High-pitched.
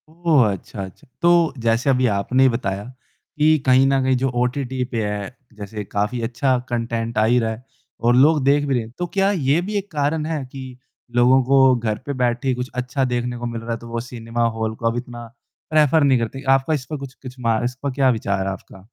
No: low, 125 Hz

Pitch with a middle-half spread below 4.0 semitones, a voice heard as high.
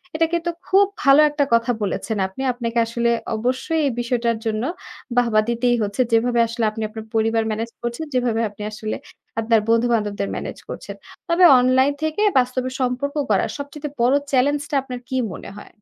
Yes: average, 2.9 semitones; high, 240 Hz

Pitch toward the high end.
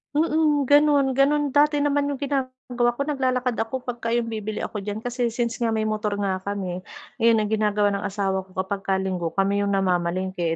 Yes: high, 225 Hz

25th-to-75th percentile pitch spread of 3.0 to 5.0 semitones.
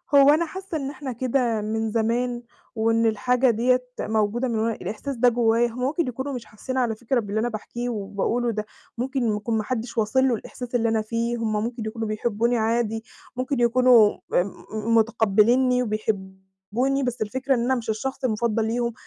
No: narrow, 2.5 semitones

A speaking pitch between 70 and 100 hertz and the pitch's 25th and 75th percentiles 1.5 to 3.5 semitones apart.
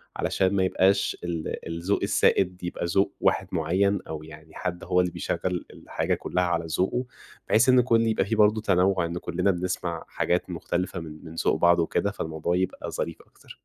Yes: very low, 90 Hz; narrow, 2.6 semitones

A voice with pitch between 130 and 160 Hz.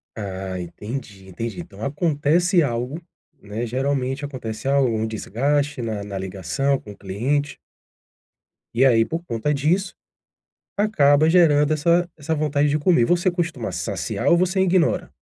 Yes: medium, 140 Hz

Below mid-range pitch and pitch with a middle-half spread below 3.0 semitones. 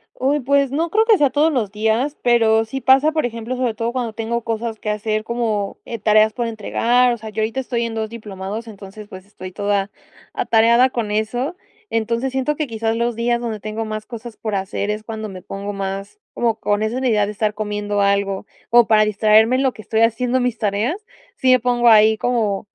No: high, 225 Hz; narrow, 2.4 semitones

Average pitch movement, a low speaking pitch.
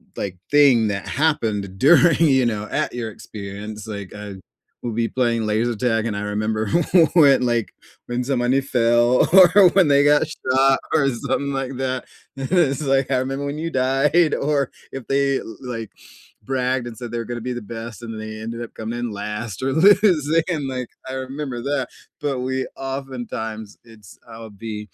Yes: average, 3.6 semitones; low, 125 Hz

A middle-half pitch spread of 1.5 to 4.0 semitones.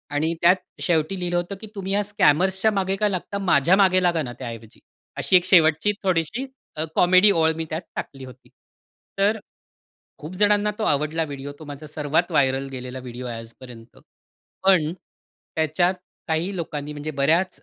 No: average, 4.7 semitones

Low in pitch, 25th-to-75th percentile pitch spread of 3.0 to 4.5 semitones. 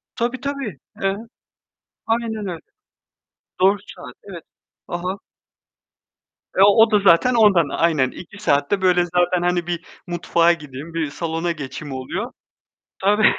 No: medium, 175 Hz; average, 3.7 semitones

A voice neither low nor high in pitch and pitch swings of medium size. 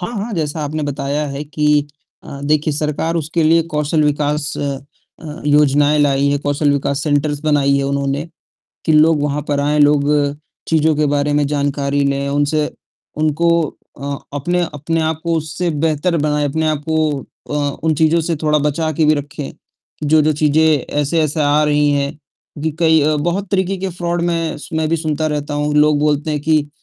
No: medium, 150 Hz; narrow, 1.6 semitones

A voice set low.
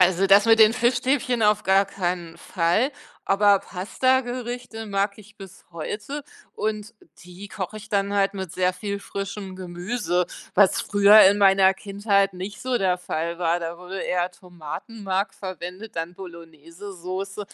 No: high, 195 Hz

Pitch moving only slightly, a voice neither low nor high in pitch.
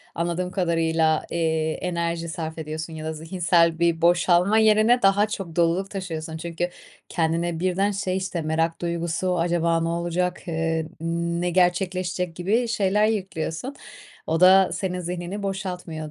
Yes: narrow, 2.3 semitones; medium, 175 Hz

